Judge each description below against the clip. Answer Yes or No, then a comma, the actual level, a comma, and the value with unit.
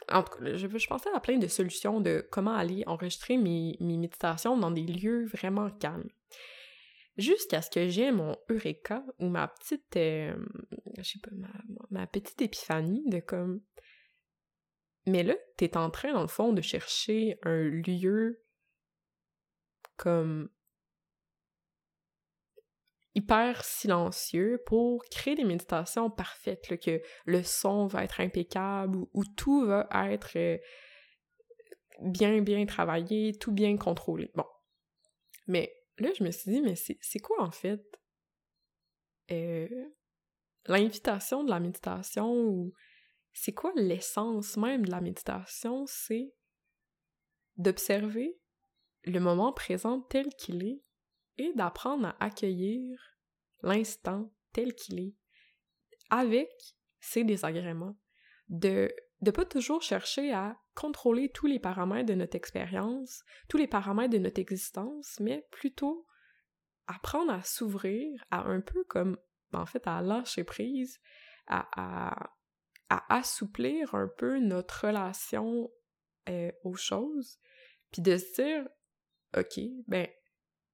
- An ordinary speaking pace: No, slow, 130 wpm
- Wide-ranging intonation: Yes, wide, 5.7 semitones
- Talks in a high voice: Yes, high, 210 Hz